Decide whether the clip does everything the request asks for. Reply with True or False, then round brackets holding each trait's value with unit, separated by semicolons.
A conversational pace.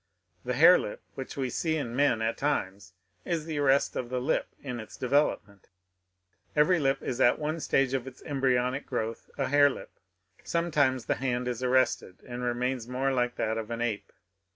True (185 wpm)